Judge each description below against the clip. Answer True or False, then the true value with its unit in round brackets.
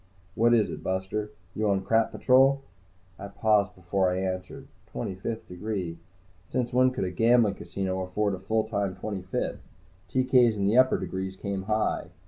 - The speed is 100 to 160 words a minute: False (170 wpm)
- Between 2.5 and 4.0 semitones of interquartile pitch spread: True (3.2 semitones)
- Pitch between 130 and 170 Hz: False (100 Hz)